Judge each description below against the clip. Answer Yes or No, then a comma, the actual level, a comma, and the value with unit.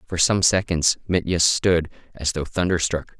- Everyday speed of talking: Yes, average, 150 wpm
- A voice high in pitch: No, very low, 90 Hz